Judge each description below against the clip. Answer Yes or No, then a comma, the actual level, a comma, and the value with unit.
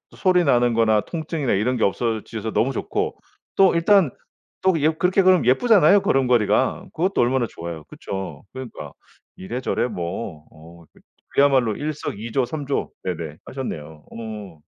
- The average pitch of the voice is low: Yes, low, 120 Hz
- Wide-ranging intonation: Yes, wide, 7.2 semitones